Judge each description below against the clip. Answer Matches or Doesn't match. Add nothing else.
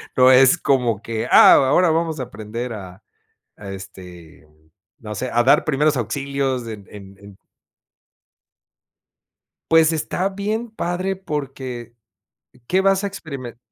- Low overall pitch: Matches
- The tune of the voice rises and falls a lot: Matches